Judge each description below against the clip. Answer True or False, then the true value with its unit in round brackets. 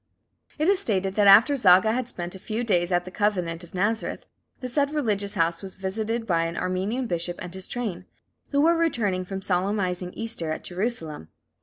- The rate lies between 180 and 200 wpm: True (190 wpm)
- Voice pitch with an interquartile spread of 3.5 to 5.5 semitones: True (4.2 semitones)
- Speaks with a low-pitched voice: False (195 Hz)